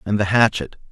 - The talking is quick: No, average, 195 wpm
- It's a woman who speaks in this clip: No, male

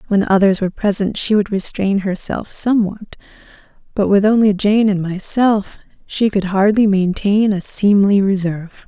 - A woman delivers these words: Yes, female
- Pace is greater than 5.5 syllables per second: No, 4.9 syllables/s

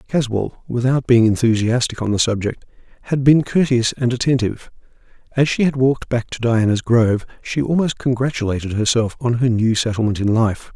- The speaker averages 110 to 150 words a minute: No, average, 165 wpm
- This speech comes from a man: Yes, male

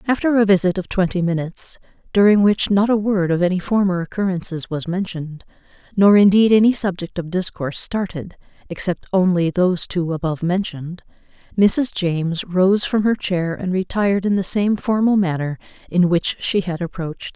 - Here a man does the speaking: No, female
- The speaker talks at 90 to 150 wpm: No, average, 165 wpm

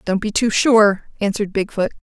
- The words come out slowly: No, fast, 205 wpm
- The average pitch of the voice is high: Yes, high, 210 Hz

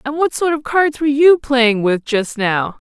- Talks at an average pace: No, fast, 230 wpm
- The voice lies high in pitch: Yes, very high, 265 Hz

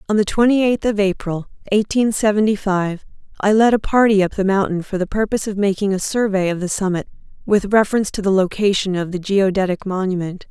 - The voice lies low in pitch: No, high, 200 Hz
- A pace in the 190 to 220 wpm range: Yes, average, 200 wpm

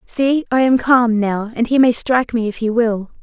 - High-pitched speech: Yes, high, 235 Hz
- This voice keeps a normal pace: No, fast, 240 wpm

